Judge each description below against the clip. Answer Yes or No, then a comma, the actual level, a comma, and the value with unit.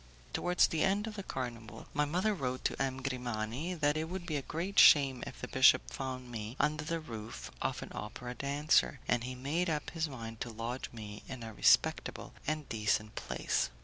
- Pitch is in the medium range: No, low, 130 Hz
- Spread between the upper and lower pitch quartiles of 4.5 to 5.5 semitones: Yes, average, 4.9 semitones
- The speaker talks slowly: No, average, 200 wpm